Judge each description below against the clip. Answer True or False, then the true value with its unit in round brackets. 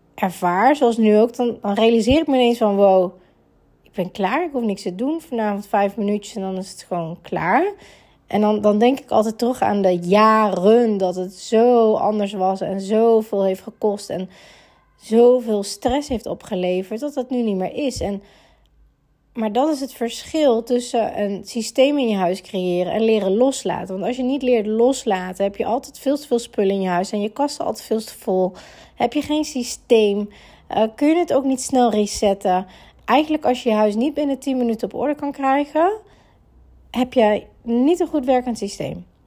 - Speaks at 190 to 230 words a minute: True (195 wpm)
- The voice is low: False (220 Hz)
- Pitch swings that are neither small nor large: True (4.3 semitones)